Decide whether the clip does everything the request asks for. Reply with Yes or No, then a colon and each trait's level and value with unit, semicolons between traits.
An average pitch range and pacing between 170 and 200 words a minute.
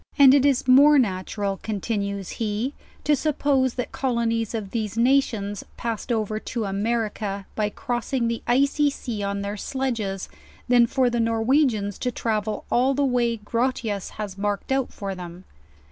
No: average, 4.0 semitones; average, 160 wpm